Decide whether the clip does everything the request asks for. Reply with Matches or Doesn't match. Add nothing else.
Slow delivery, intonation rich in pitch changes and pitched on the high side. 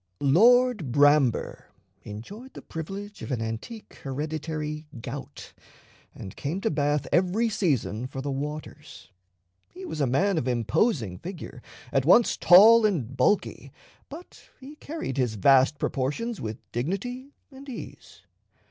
Doesn't match